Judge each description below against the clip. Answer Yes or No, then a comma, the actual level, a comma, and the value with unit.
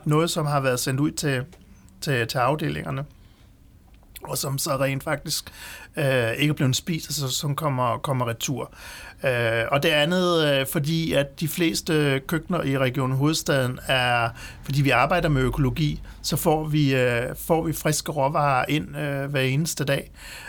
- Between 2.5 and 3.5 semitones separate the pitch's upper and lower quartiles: Yes, average, 3.2 semitones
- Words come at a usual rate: Yes, average, 175 wpm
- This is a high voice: No, medium, 140 Hz